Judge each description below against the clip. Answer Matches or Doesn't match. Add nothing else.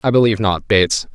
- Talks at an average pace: Doesn't match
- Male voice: Matches